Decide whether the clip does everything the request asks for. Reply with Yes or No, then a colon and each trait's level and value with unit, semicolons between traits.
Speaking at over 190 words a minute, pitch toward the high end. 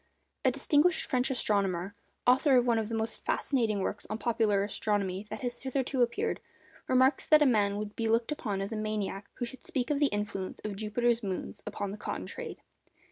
Yes: average, 200 wpm; high, 225 Hz